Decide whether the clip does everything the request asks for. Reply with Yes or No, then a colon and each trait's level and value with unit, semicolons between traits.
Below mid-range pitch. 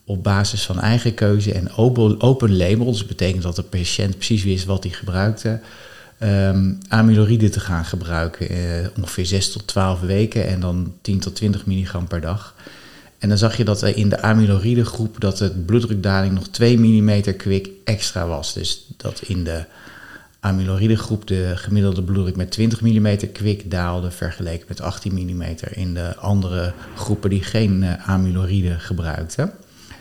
Yes: low, 100 Hz